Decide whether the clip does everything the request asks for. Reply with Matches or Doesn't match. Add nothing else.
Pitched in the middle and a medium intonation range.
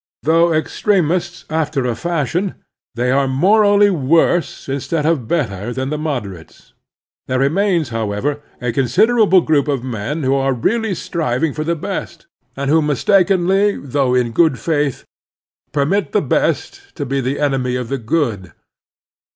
Matches